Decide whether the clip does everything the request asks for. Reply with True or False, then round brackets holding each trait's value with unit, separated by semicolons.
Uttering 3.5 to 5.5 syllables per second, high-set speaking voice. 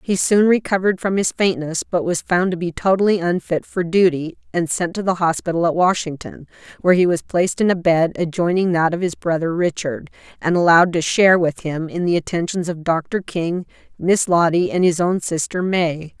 False (5.3 syllables/s; 175 Hz)